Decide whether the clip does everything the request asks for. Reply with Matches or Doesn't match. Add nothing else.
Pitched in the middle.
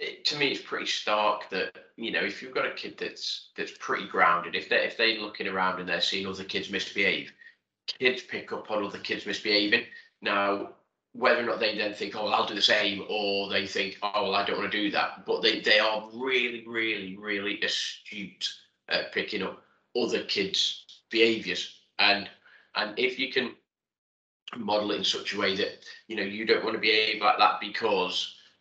Doesn't match